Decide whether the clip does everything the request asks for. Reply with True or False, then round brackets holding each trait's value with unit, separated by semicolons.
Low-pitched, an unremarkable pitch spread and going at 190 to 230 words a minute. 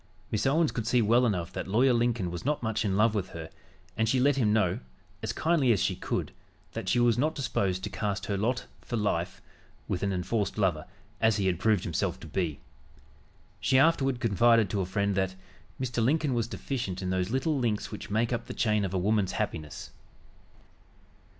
True (110 Hz; 4.3 semitones; 200 wpm)